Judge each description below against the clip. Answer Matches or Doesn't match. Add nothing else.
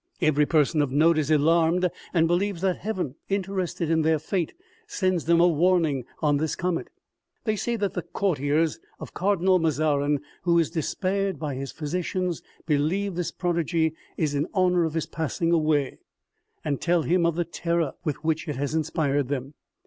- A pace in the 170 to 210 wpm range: Matches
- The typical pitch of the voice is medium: Matches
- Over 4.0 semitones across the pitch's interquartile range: Doesn't match